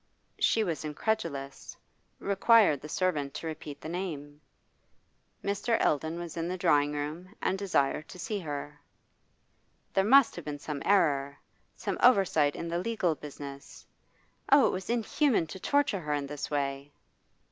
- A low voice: No, medium, 165 Hz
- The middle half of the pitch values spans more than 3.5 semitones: Yes, average, 5.1 semitones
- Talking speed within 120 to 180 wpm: Yes, average, 150 wpm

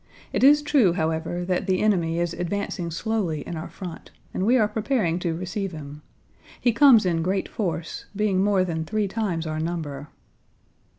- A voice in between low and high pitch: Yes, medium, 180 Hz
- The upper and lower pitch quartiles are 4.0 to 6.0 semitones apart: Yes, average, 4.3 semitones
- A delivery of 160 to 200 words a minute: Yes, average, 175 wpm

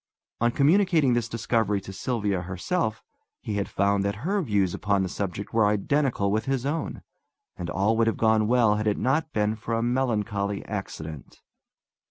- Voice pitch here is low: Yes, low, 110 Hz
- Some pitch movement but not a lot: Yes, average, 3.8 semitones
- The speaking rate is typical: Yes, average, 175 wpm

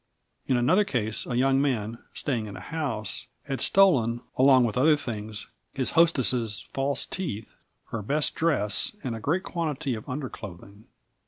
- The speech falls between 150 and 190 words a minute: Yes, average, 155 wpm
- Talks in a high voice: No, low, 130 Hz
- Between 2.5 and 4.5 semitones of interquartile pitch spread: No, average, 5.0 semitones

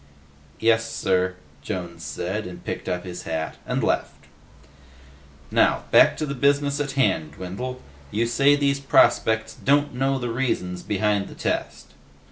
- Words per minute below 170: Yes, average, 145 wpm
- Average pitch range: No, wide, 7.0 semitones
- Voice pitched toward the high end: No, low, 110 Hz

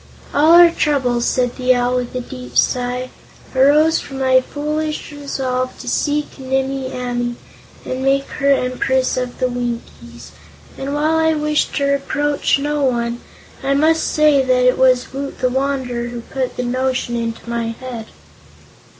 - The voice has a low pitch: No, very high, 260 Hz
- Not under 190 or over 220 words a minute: No, average, 160 wpm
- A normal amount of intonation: No, narrow, 2.3 semitones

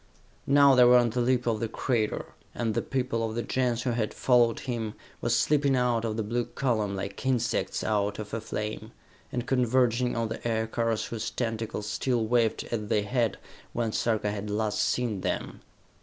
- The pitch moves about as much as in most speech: No, narrow, 2.3 semitones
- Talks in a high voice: No, low, 115 Hz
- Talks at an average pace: Yes, average, 185 wpm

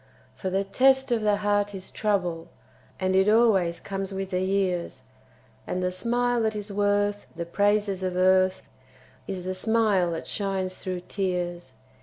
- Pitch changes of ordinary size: No, narrow, 2.0 semitones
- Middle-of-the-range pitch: No, high, 195 Hz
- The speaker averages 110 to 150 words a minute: No, average, 160 wpm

